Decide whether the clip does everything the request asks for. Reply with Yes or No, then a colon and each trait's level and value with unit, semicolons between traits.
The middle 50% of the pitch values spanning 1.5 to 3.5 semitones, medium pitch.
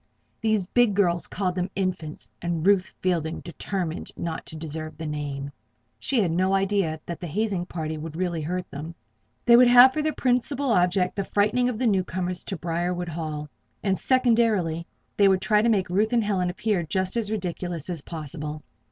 No: average, 4.1 semitones; medium, 180 Hz